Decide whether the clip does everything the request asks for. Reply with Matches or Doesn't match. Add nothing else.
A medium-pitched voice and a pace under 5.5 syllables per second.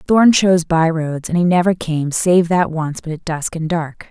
Matches